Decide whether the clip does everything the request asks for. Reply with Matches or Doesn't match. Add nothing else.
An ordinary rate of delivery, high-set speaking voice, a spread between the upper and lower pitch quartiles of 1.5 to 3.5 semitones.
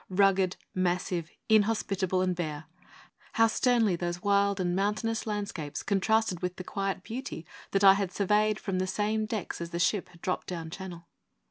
Matches